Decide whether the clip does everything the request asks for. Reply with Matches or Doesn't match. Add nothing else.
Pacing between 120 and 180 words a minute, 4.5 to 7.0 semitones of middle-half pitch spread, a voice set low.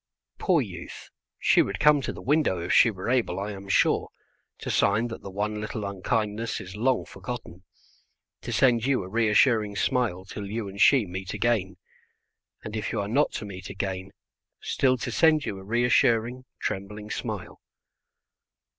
Doesn't match